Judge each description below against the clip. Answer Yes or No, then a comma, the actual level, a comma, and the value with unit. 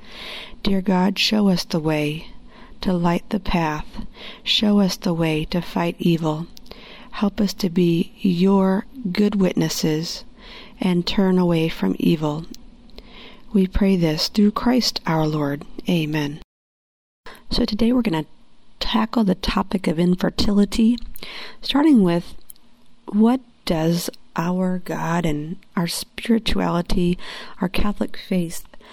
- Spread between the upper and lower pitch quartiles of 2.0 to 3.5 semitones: No, average, 4.5 semitones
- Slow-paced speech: Yes, slow, 120 wpm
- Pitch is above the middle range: Yes, high, 195 Hz